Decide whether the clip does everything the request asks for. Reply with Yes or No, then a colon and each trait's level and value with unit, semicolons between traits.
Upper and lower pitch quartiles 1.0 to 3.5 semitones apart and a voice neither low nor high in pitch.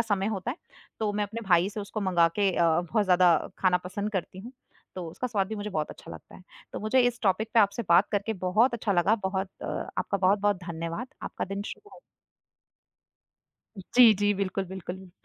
No: narrow, 2.6 semitones; high, 200 Hz